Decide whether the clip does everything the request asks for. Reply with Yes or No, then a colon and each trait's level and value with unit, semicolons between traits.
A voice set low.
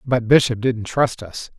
Yes: low, 120 Hz